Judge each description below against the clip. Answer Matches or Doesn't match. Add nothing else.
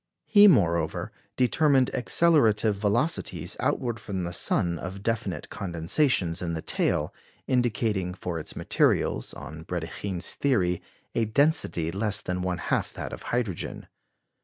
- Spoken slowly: Matches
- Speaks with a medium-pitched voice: Doesn't match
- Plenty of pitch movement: Matches